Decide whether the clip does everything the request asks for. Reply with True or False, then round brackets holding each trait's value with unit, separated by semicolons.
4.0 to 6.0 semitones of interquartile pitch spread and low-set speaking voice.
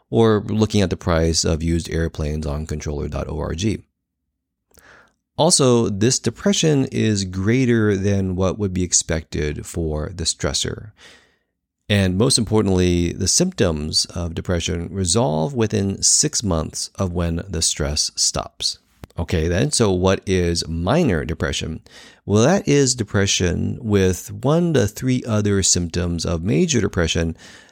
True (4.8 semitones; 95 Hz)